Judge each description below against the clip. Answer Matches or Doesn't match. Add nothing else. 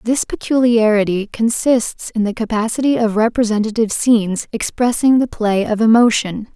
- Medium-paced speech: Doesn't match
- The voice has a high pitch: Matches